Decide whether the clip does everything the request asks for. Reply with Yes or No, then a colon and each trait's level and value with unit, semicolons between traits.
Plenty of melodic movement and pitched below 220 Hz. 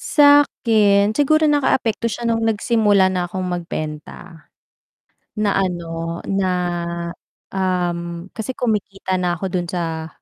No: average, 4.4 semitones; high, 190 Hz